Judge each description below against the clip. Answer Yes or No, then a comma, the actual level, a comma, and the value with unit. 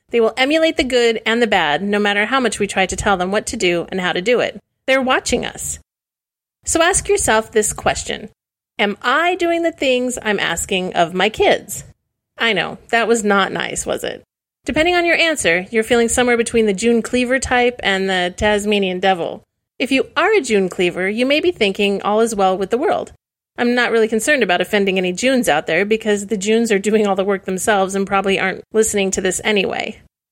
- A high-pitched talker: Yes, high, 220 Hz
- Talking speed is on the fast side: Yes, fast, 215 wpm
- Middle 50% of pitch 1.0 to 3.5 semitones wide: No, average, 4.2 semitones